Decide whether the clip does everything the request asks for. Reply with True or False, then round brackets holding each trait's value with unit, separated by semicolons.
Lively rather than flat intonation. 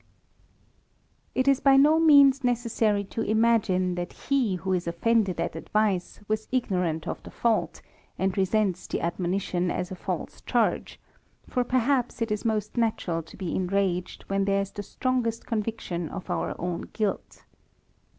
False (4.3 semitones)